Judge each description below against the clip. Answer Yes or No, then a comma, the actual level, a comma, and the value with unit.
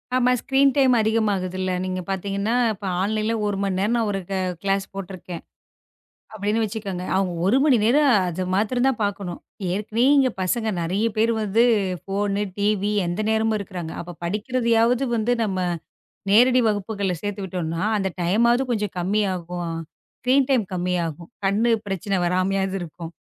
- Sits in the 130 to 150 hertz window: No, high, 200 Hz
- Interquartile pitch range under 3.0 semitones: No, average, 3.4 semitones